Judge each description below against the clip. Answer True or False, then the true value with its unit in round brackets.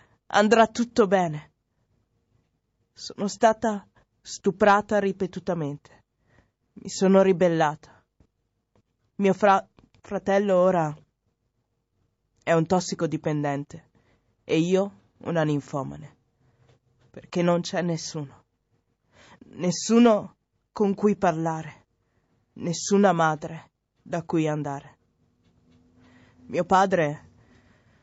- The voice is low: False (165 Hz)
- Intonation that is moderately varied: False (7.4 semitones)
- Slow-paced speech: True (75 wpm)